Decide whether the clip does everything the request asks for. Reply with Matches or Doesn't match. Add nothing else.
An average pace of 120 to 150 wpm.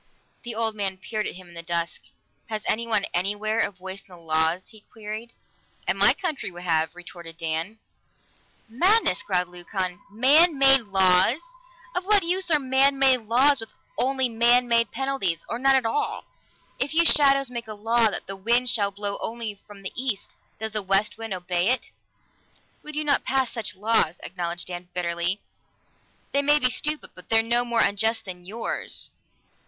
Doesn't match